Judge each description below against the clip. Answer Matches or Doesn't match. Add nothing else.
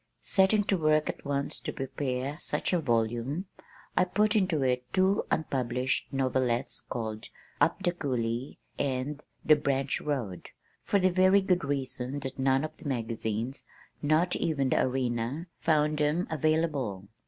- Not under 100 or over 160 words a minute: Matches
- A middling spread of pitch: Matches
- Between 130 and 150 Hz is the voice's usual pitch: Matches